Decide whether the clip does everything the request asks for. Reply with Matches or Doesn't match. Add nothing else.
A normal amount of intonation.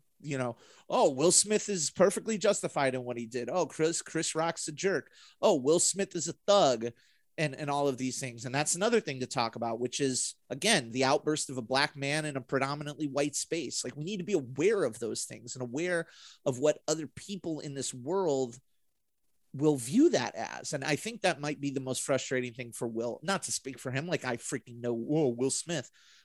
Matches